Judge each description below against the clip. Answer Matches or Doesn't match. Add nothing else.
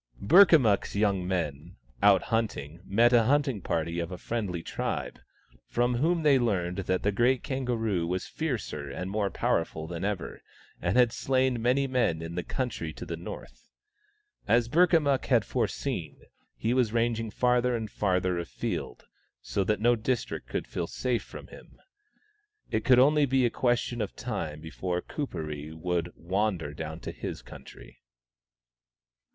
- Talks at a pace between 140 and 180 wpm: Matches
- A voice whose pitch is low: Matches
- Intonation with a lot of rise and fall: Matches